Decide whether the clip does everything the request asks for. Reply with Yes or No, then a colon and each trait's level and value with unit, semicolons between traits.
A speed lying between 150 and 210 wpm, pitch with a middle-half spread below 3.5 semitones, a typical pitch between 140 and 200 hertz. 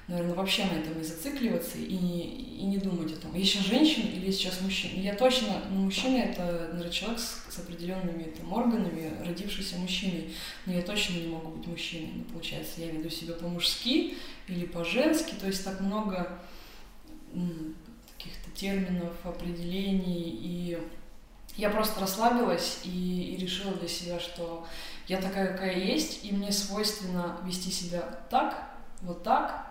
Yes: average, 155 wpm; average, 2.9 semitones; medium, 185 Hz